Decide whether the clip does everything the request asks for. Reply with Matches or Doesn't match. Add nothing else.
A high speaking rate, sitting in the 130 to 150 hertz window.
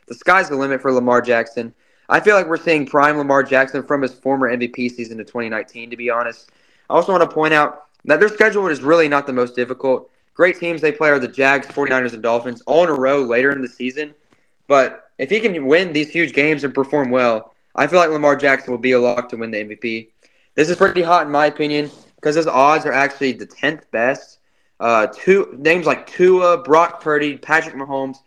Matches